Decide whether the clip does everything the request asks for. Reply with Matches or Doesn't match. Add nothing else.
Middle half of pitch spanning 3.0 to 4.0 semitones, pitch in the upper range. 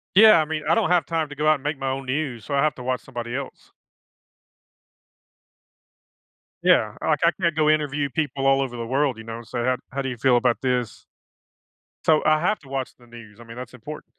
Doesn't match